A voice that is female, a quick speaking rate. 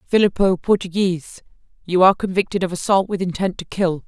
No: female; average, 160 wpm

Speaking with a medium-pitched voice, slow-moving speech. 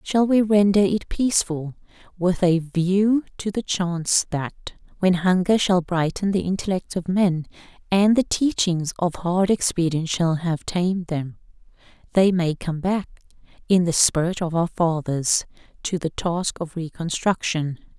No: medium, 180 Hz; average, 150 wpm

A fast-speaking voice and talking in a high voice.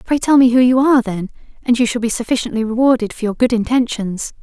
Yes: fast, 230 wpm; high, 235 Hz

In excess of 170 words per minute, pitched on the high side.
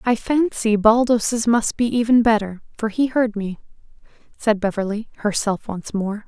No: average, 155 wpm; high, 220 Hz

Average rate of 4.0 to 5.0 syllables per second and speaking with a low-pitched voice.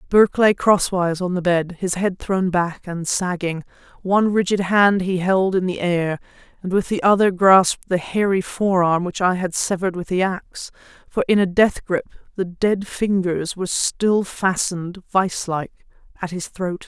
No: 4.6 syllables/s; medium, 185 Hz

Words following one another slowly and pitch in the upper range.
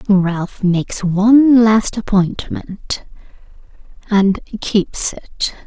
Yes: slow, 75 wpm; high, 200 Hz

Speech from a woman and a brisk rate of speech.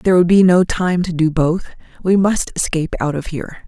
Yes: female; fast, 230 wpm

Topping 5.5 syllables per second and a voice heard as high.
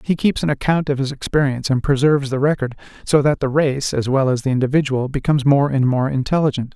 No: 6.3 syllables/s; medium, 140 Hz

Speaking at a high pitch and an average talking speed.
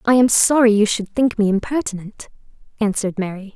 Yes: high, 215 Hz; average, 170 wpm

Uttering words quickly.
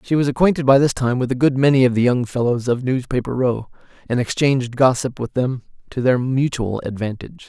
Yes: fast, 210 wpm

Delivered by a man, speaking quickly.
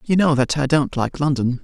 Yes: male; fast, 255 wpm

